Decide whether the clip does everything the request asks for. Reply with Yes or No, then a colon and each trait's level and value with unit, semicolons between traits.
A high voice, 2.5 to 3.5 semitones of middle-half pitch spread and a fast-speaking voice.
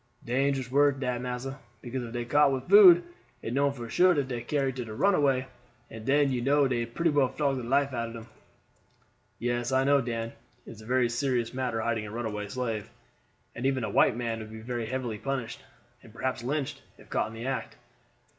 No: low, 125 Hz; average, 2.8 semitones; fast, 210 wpm